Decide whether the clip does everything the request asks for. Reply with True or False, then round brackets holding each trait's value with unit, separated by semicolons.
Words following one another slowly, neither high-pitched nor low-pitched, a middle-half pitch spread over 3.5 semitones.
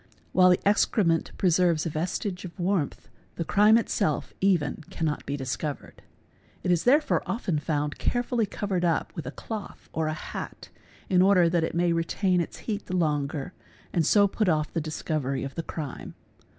False (175 wpm; 170 Hz; 3.9 semitones)